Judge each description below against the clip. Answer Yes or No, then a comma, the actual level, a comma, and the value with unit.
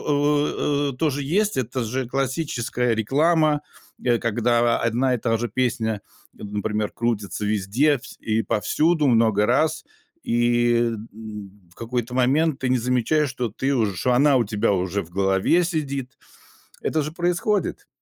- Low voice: Yes, low, 125 Hz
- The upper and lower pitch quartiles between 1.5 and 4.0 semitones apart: No, average, 4.5 semitones